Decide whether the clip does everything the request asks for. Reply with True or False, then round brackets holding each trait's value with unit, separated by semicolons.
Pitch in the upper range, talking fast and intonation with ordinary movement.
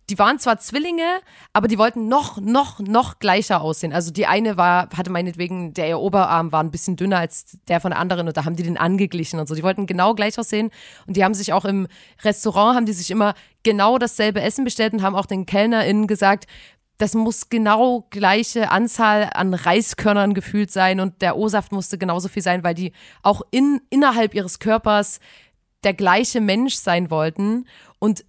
True (200 Hz; 195 wpm; 3.2 semitones)